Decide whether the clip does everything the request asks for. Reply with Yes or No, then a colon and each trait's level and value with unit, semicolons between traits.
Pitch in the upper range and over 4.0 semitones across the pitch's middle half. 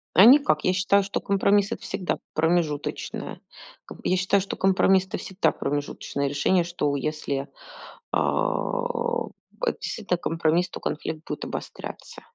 No: medium, 180 Hz; average, 4.4 semitones